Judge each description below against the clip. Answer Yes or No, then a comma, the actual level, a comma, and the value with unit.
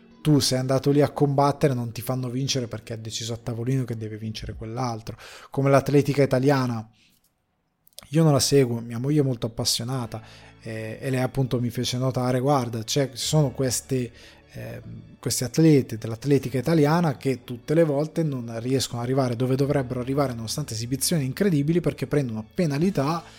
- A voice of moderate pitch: No, low, 130 Hz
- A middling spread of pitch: Yes, average, 3.4 semitones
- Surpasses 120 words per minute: Yes, average, 160 wpm